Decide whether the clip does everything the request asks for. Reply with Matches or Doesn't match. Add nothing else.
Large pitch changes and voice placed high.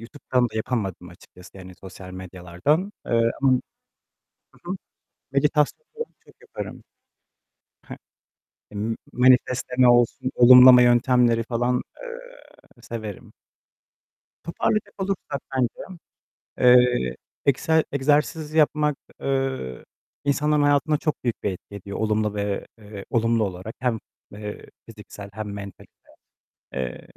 Doesn't match